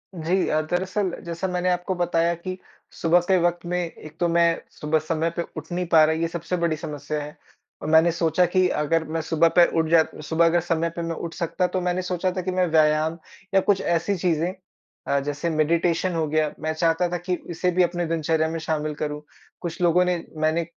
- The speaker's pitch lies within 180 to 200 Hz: No, medium, 170 Hz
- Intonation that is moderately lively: No, narrow, 2.0 semitones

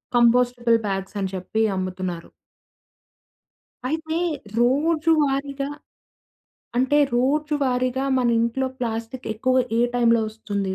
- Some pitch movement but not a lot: Yes, average, 3.4 semitones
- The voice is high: Yes, high, 245 Hz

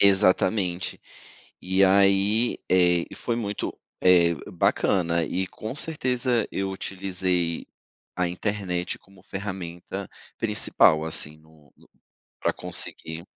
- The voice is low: Yes, very low, 95 Hz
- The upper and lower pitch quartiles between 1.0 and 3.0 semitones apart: Yes, narrow, 2.6 semitones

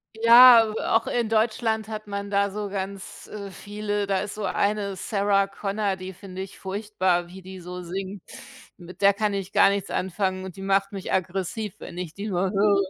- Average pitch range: No, narrow, 1.8 semitones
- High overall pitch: Yes, high, 200 Hz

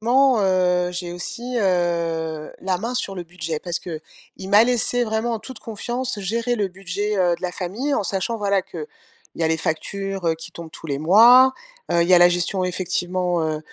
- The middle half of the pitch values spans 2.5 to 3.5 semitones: No, average, 4.1 semitones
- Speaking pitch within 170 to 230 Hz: Yes, medium, 185 Hz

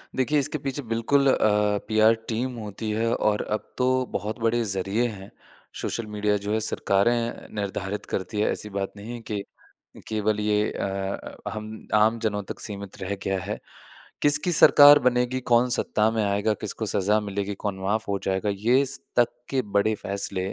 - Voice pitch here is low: Yes, low, 105 Hz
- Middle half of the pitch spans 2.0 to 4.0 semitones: Yes, average, 2.9 semitones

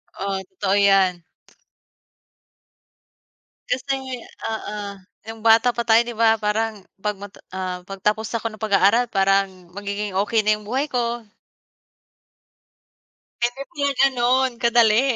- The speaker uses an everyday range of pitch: Yes, average, 3.2 semitones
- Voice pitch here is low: No, high, 220 Hz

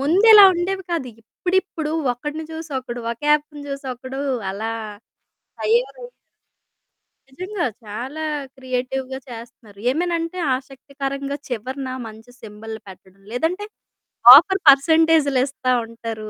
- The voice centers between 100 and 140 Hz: No, very high, 275 Hz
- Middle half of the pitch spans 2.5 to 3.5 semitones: No, average, 5.1 semitones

